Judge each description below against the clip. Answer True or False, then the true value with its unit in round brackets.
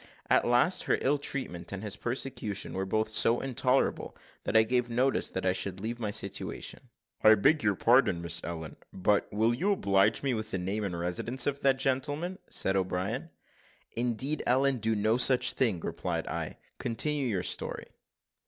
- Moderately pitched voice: False (115 Hz)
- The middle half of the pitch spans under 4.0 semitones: False (5.1 semitones)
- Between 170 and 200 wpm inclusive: True (175 wpm)